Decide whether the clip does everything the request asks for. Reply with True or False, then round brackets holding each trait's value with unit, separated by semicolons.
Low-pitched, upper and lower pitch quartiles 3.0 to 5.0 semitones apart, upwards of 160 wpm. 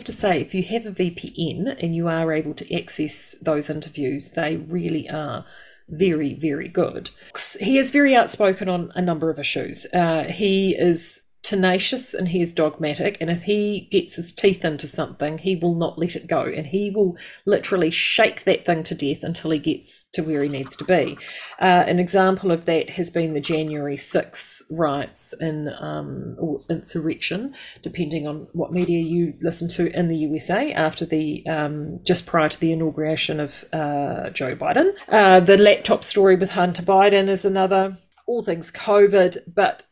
False (170 Hz; 3.4 semitones; 180 wpm)